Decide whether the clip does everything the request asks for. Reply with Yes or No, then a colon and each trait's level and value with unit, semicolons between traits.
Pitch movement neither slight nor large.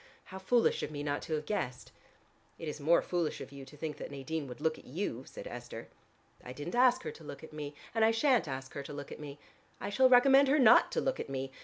No: wide, 8.0 semitones